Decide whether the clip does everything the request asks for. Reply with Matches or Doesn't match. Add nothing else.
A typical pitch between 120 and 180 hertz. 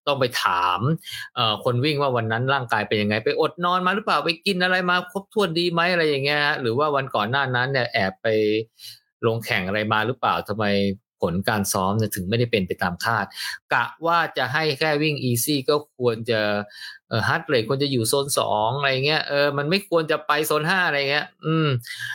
Matches